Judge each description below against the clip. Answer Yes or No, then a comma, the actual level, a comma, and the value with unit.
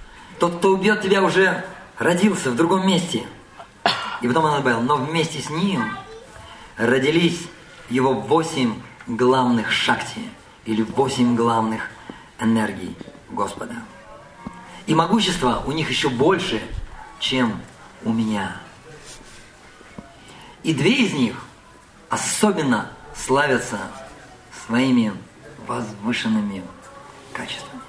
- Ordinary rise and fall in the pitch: No, wide, 7.4 semitones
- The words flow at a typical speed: No, slow, 95 wpm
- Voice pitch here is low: No, medium, 150 Hz